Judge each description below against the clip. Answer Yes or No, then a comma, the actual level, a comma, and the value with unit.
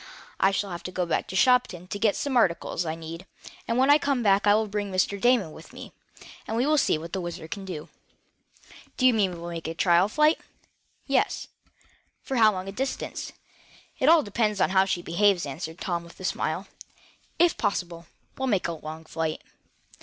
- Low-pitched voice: No, high, 195 Hz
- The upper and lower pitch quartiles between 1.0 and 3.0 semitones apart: No, average, 5.2 semitones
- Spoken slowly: No, fast, 205 wpm